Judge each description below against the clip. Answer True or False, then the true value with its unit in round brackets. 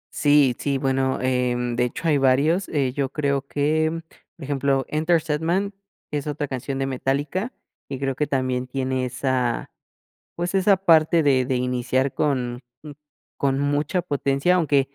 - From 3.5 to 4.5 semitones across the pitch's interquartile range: False (3.0 semitones)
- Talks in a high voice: False (140 Hz)